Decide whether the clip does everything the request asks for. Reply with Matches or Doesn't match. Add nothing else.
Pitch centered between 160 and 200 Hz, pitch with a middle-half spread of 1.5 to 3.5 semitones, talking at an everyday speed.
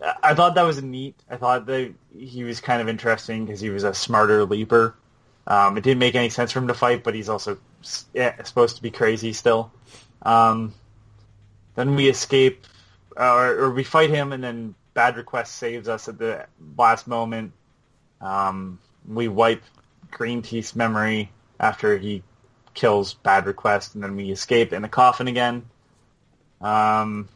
Doesn't match